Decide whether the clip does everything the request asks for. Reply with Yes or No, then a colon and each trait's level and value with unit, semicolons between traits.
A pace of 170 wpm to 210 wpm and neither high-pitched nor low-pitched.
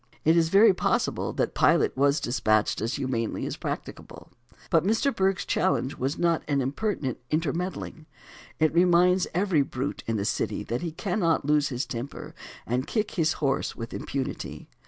No: average, 160 wpm; medium, 155 Hz